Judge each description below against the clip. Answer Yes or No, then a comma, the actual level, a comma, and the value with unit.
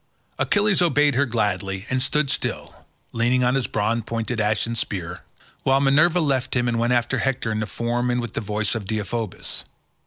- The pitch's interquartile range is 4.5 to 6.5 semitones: No, average, 3.6 semitones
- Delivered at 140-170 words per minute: No, average, 185 wpm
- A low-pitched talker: Yes, low, 120 Hz